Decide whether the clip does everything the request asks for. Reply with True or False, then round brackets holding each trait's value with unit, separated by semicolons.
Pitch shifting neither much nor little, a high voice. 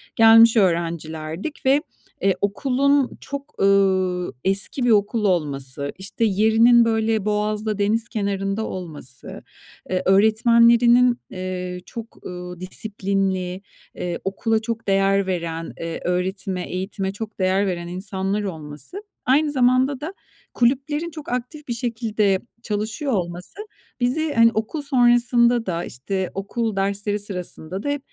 True (4.3 semitones; 205 Hz)